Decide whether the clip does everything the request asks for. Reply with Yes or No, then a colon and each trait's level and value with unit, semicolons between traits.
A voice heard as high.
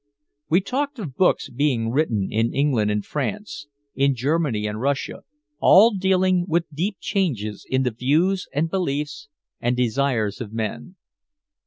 No: medium, 140 Hz